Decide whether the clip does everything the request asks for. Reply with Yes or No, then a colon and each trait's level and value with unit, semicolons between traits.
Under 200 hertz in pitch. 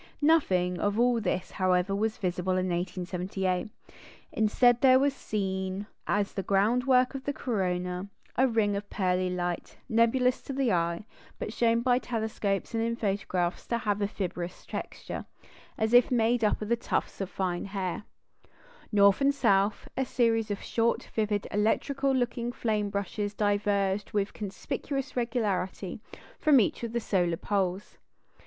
No: high, 205 Hz